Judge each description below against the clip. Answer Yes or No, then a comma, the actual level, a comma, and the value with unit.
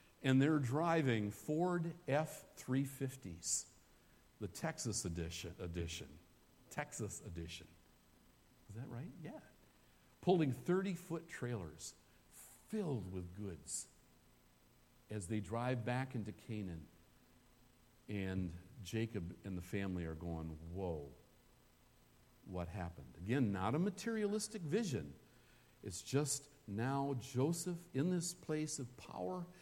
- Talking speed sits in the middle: No, slow, 105 wpm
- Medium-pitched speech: No, low, 115 Hz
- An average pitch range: No, wide, 8.9 semitones